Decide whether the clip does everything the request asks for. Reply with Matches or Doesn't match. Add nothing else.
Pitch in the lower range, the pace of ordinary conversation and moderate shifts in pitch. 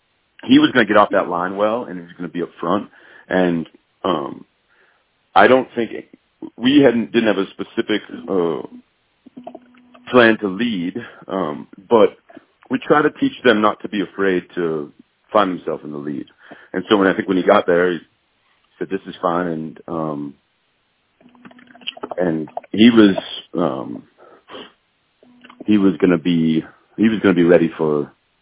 Doesn't match